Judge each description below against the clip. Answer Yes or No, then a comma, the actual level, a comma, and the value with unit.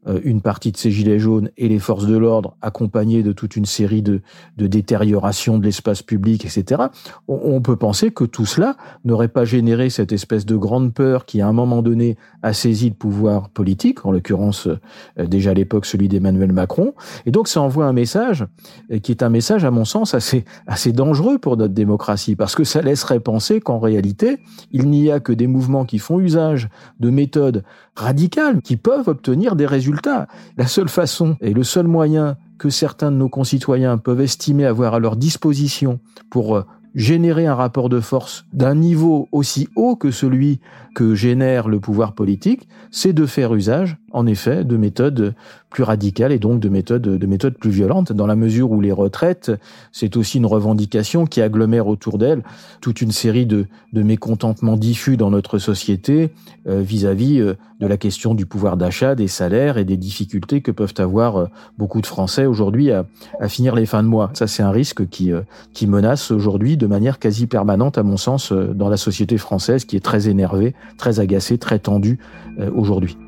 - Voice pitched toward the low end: Yes, low, 115 Hz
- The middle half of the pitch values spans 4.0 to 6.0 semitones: Yes, average, 4.3 semitones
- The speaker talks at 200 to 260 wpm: No, average, 190 wpm